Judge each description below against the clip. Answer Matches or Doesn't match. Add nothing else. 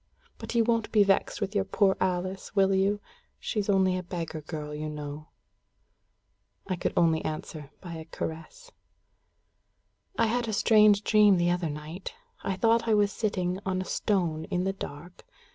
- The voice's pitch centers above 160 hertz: Matches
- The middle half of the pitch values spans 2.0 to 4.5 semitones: Matches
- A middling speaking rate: Matches